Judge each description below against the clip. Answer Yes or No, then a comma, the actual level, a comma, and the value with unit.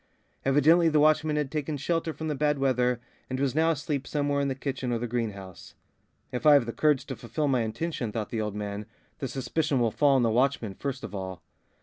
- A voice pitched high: No, low, 135 Hz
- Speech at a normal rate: No, fast, 225 wpm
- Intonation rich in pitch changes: No, average, 4.2 semitones